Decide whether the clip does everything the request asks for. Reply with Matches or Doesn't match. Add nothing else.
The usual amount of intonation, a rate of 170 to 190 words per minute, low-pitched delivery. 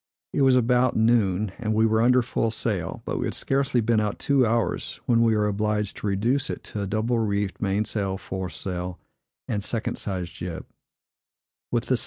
Matches